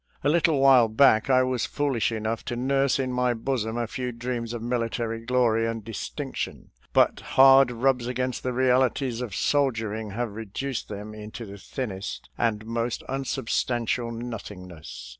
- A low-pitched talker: Yes, low, 120 Hz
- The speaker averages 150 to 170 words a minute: Yes, average, 155 wpm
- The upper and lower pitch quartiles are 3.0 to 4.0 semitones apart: No, narrow, 2.4 semitones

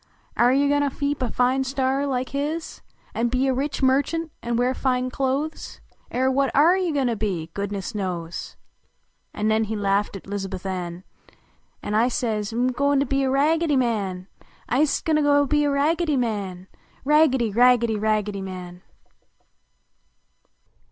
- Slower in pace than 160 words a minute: No, average, 175 wpm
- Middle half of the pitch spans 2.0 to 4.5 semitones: No, average, 5.2 semitones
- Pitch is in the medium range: No, very high, 250 Hz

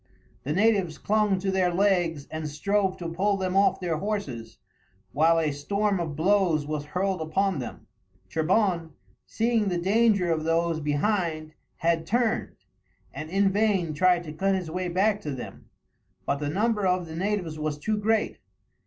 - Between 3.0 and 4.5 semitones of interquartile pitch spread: Yes, average, 4.2 semitones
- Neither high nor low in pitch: Yes, medium, 180 Hz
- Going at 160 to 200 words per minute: Yes, average, 165 wpm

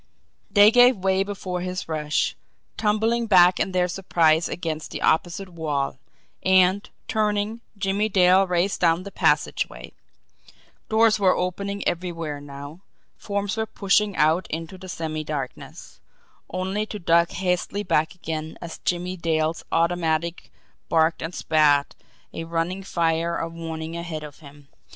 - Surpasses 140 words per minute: No, slow, 135 wpm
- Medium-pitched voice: Yes, medium, 175 Hz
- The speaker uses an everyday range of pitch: Yes, average, 3.2 semitones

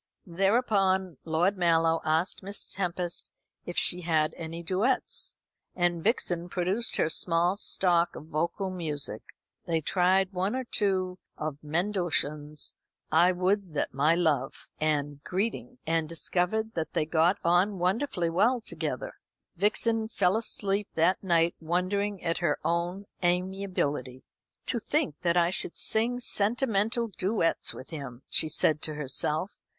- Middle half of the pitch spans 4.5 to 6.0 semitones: No, average, 3.4 semitones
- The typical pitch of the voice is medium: Yes, medium, 175 Hz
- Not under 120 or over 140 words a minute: Yes, slow, 135 wpm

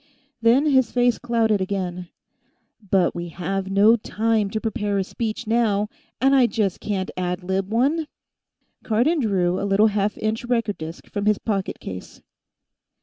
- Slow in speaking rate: No, average, 155 wpm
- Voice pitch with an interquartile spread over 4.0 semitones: No, average, 3.3 semitones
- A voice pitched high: Yes, high, 210 Hz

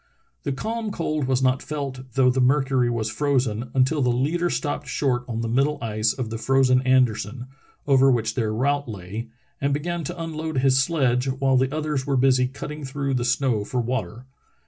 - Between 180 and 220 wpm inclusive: Yes, average, 190 wpm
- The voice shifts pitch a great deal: No, narrow, 2.6 semitones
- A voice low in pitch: Yes, low, 130 Hz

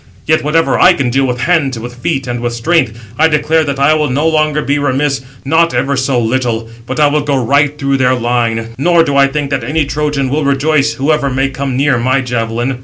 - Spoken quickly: Yes, fast, 225 wpm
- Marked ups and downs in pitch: No, average, 3.1 semitones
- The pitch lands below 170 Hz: Yes, medium, 140 Hz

